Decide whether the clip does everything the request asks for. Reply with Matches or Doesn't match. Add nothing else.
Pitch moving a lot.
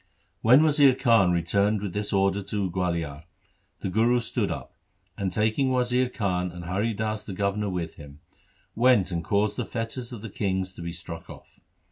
Doesn't match